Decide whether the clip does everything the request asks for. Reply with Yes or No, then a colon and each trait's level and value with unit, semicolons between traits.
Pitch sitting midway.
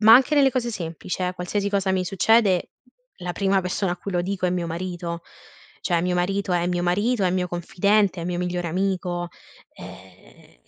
Yes: medium, 180 Hz